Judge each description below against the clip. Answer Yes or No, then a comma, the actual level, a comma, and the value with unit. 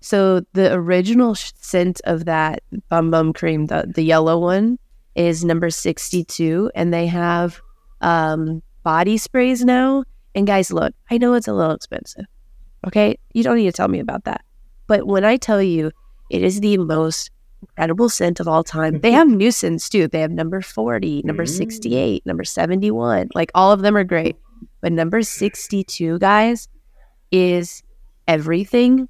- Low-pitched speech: No, medium, 180 Hz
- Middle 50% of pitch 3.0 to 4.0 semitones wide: No, average, 4.4 semitones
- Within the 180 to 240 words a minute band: No, average, 165 wpm